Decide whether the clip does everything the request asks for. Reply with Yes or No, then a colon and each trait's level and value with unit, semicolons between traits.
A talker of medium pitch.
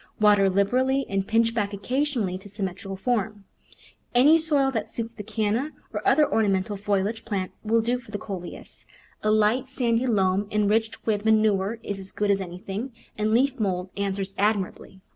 No: high, 210 Hz